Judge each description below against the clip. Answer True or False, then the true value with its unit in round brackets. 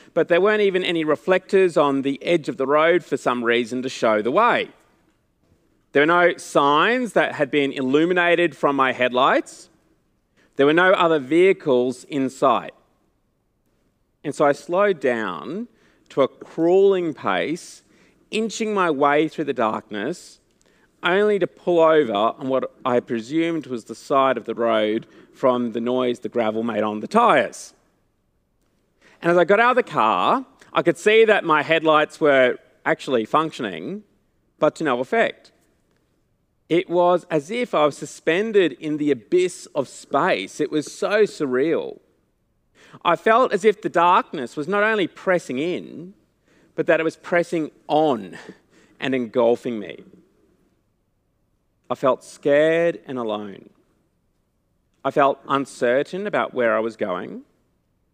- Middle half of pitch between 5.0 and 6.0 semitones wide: True (5.5 semitones)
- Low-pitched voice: False (155 Hz)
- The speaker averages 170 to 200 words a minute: False (150 wpm)